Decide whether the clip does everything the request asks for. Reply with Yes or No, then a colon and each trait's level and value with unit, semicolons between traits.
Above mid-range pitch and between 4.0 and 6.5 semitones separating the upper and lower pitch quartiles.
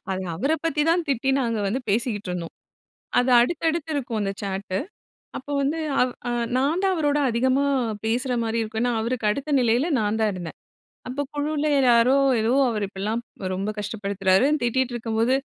Yes: high, 235 Hz; average, 4.7 semitones